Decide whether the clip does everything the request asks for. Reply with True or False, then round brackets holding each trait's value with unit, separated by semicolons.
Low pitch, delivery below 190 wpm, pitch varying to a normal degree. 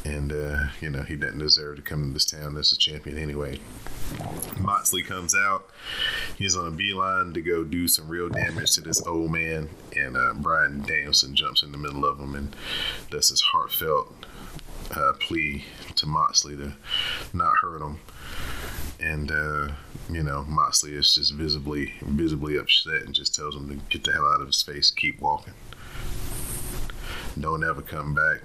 True (75 Hz; 175 wpm; 3.2 semitones)